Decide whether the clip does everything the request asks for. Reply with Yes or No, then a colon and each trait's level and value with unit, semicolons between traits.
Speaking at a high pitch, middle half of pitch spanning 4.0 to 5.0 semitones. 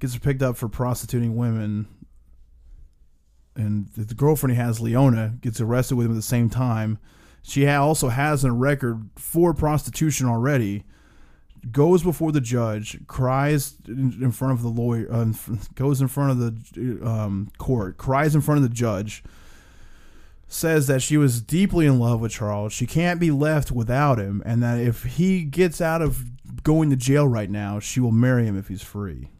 No: low, 120 Hz; average, 4.5 semitones